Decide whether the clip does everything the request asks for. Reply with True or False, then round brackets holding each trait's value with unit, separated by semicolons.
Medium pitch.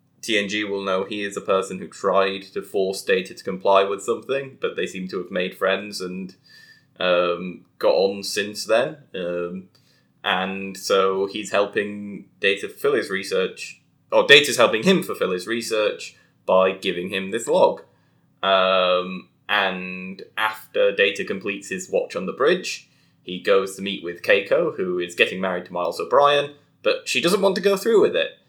False (100 Hz)